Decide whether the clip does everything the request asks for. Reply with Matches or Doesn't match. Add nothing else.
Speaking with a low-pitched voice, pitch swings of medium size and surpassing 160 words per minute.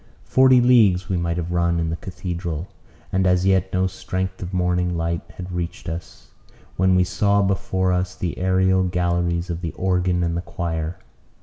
Doesn't match